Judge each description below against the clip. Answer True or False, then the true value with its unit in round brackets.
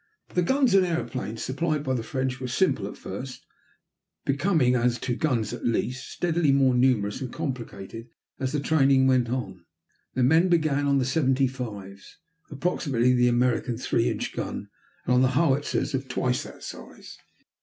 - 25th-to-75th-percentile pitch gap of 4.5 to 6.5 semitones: False (2.9 semitones)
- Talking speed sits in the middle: True (165 wpm)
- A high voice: False (130 Hz)